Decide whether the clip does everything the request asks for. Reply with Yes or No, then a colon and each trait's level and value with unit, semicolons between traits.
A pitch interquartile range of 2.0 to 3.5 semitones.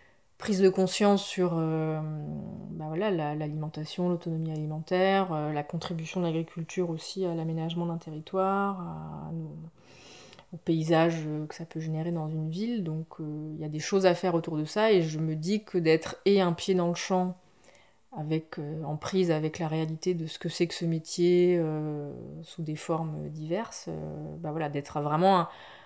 Yes: average, 2.7 semitones